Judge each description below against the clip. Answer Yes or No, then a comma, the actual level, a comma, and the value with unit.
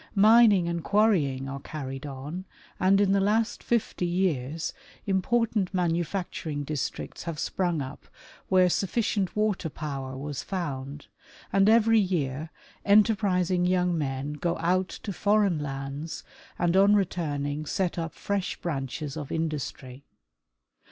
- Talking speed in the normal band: No, slow, 130 wpm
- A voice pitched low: No, medium, 175 Hz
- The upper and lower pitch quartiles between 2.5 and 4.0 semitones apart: No, average, 5.2 semitones